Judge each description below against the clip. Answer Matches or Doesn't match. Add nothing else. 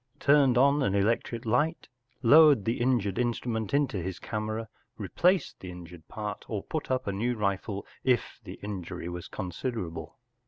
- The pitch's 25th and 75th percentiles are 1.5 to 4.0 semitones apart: Doesn't match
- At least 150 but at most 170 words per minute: Matches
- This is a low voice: Matches